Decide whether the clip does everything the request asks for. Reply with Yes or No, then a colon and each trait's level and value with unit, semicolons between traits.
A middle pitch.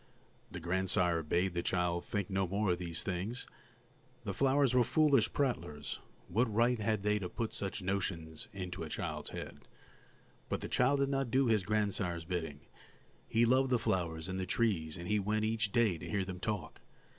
No: low, 100 Hz